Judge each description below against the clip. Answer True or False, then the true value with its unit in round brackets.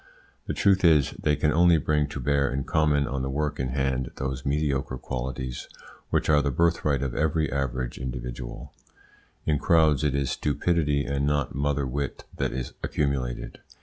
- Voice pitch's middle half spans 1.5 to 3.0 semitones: True (2.4 semitones)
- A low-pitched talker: True (70 Hz)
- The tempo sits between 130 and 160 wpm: False (170 wpm)